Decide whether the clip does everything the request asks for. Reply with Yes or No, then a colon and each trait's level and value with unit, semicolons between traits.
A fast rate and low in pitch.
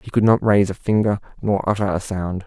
Yes: fast, 245 wpm; low, 100 Hz